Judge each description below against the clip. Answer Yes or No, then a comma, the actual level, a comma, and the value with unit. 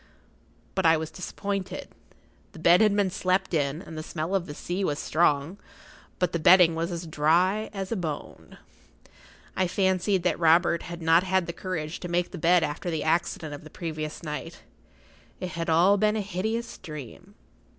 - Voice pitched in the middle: Yes, medium, 175 Hz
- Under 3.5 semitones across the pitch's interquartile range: Yes, average, 2.8 semitones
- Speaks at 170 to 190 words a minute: Yes, average, 180 wpm